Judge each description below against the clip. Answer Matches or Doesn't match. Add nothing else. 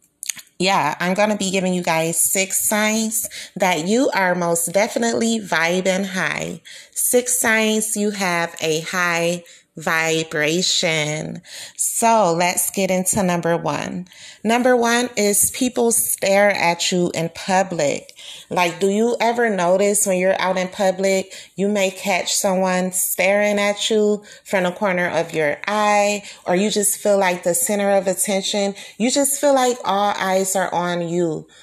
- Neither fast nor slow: Matches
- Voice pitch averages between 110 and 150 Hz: Doesn't match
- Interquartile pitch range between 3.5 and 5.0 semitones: Doesn't match